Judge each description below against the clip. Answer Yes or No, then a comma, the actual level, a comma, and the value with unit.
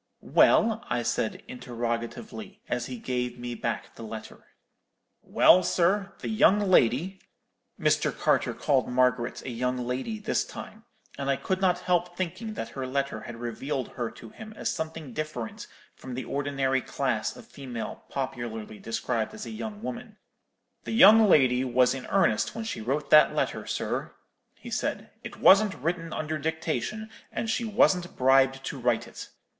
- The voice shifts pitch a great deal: Yes, wide, 7.5 semitones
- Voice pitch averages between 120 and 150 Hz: Yes, medium, 140 Hz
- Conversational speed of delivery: Yes, average, 160 wpm